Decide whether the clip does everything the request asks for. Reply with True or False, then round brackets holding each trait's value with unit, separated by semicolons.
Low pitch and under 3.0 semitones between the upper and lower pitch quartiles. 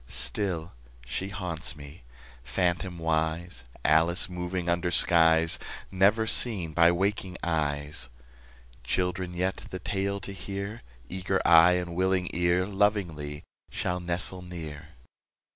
True (90 Hz; 2.5 semitones)